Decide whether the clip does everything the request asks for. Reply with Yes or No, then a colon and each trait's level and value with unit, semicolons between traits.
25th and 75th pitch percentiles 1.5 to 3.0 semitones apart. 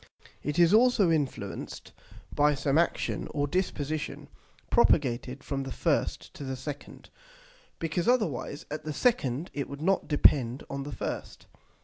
No: average, 3.5 semitones